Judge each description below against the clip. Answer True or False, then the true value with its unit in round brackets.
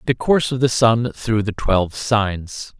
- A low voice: True (115 Hz)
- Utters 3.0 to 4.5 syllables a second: True (4.2 syllables/s)